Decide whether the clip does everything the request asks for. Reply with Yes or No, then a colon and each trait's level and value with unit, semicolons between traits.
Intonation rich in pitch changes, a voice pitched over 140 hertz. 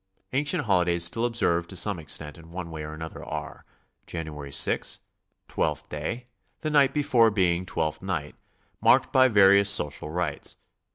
No: wide, 6.0 semitones; very low, 90 Hz